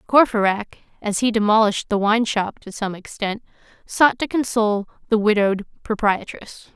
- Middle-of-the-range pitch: No, high, 215 Hz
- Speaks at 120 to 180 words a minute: Yes, average, 140 wpm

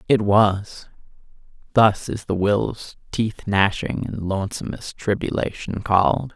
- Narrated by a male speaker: Yes, male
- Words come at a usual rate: No, slow, 115 wpm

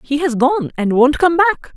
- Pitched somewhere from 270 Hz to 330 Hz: Yes, very high, 290 Hz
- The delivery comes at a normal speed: No, fast, 240 wpm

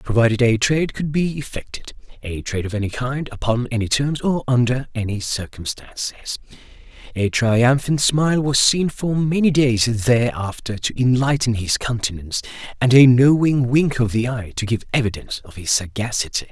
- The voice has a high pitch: No, low, 125 Hz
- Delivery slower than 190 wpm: Yes, average, 155 wpm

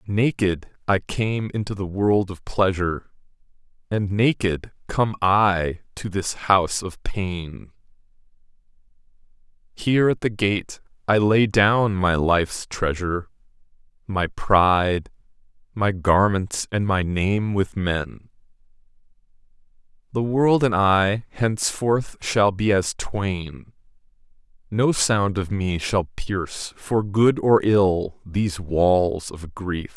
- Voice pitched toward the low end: Yes, low, 100 Hz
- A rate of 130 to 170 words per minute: No, slow, 120 wpm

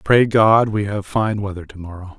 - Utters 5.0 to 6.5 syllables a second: No, 4.8 syllables/s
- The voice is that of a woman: No, male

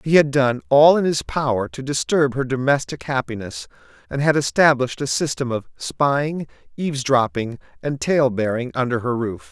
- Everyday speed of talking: Yes, average, 160 wpm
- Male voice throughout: Yes, male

